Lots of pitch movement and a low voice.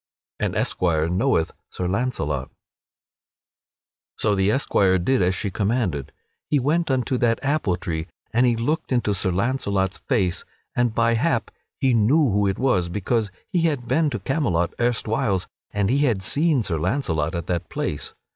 Yes: wide, 6.0 semitones; low, 105 Hz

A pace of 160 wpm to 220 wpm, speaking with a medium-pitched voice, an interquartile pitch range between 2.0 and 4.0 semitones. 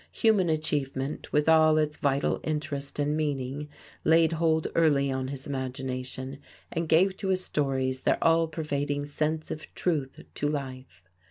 No: average, 150 wpm; medium, 150 Hz; average, 2.9 semitones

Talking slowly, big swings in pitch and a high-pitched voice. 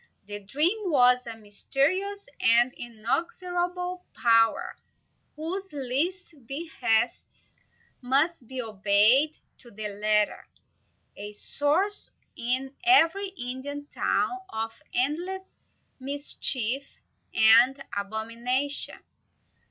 Yes: slow, 85 wpm; wide, 6.7 semitones; very high, 265 Hz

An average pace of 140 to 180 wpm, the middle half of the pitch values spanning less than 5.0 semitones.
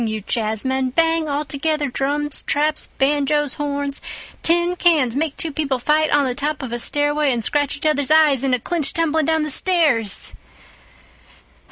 Yes: average, 160 wpm; narrow, 2.5 semitones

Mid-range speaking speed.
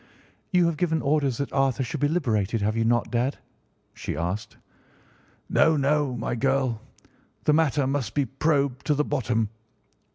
Yes: average, 160 wpm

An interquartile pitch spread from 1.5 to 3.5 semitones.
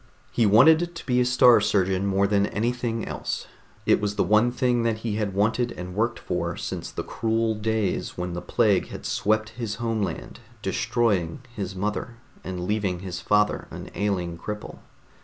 Yes: average, 3.0 semitones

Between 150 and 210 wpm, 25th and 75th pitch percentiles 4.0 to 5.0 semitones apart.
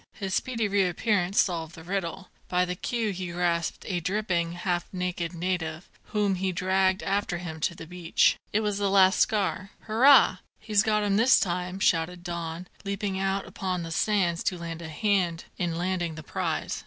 No: average, 175 wpm; narrow, 2.6 semitones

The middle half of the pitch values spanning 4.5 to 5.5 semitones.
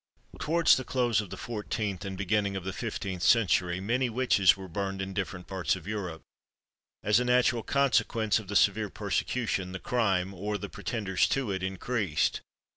No: average, 3.6 semitones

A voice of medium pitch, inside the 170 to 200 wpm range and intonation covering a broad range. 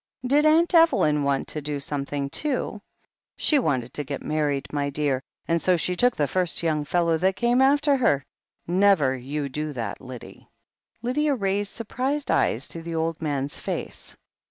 Yes: medium, 165 Hz; average, 175 wpm; wide, 8.9 semitones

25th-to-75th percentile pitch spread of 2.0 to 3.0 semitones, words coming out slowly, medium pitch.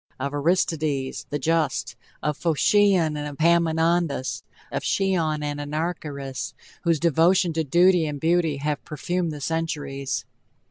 Yes: average, 2.7 semitones; slow, 125 wpm; medium, 160 Hz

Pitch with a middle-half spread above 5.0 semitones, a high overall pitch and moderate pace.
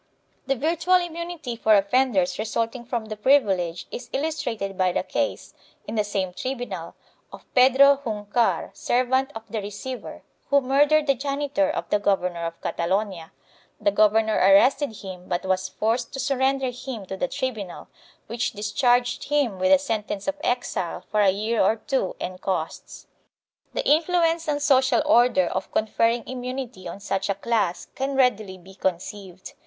Yes: wide, 5.5 semitones; high, 230 Hz; average, 160 wpm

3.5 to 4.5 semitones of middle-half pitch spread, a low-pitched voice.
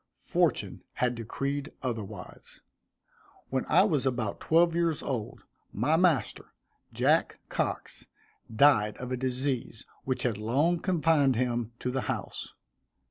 Yes: average, 4.1 semitones; low, 130 Hz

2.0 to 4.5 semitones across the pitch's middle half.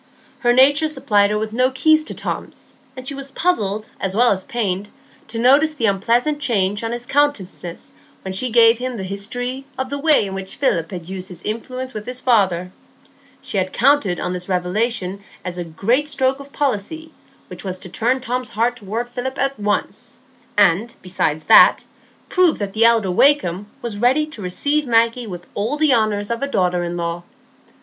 No: average, 5.3 semitones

